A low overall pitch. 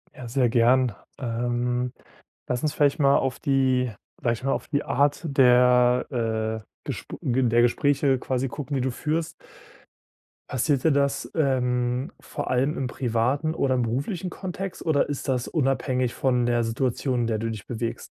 Yes: low, 130 Hz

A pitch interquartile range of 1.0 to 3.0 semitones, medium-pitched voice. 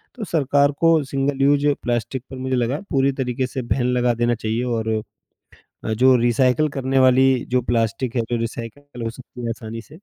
No: narrow, 2.6 semitones; low, 125 Hz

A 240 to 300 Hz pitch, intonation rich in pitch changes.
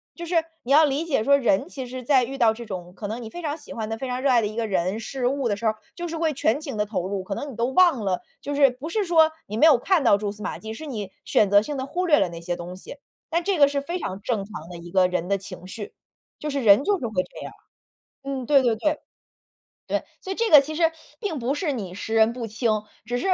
Yes: high, 245 Hz; wide, 6.1 semitones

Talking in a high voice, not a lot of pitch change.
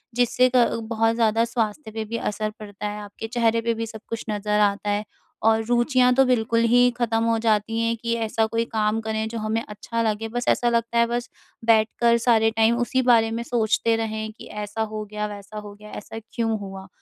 Yes: high, 225 Hz; narrow, 1.5 semitones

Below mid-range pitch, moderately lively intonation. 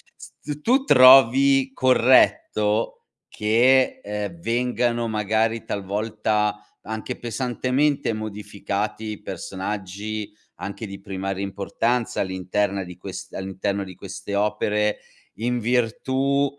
Yes: low, 105 Hz; average, 3.6 semitones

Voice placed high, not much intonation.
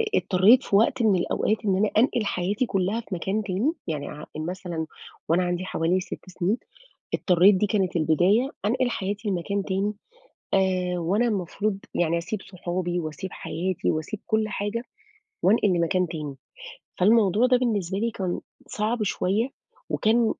No: high, 195 Hz; average, 3.3 semitones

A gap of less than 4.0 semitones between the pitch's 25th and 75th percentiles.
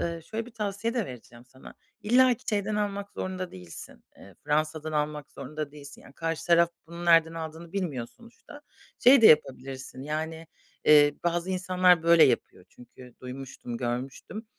No: wide, 5.5 semitones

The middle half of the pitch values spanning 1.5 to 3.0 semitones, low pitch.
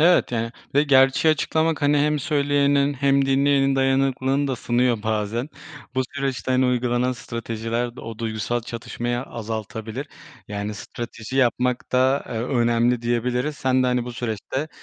Yes: average, 2.7 semitones; low, 125 Hz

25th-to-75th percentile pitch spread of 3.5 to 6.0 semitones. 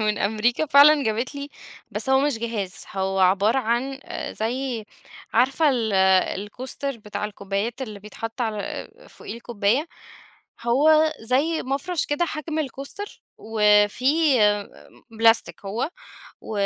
Yes: average, 4.7 semitones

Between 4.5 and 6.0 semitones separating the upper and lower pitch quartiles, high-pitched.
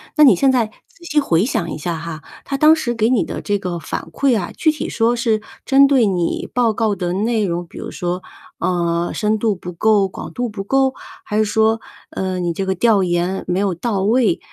Yes: average, 5.1 semitones; high, 210 Hz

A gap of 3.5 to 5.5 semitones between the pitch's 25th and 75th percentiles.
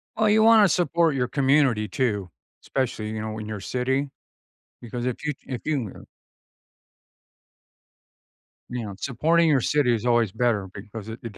Yes: average, 5.2 semitones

